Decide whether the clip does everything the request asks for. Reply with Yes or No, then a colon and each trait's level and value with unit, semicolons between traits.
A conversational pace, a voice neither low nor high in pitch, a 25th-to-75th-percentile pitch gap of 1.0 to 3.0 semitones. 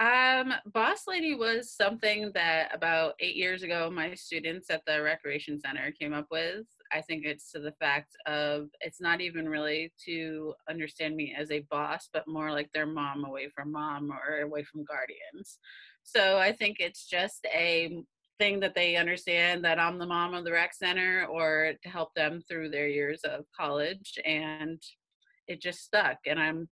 Yes: average, 180 wpm; medium, 160 Hz; average, 2.7 semitones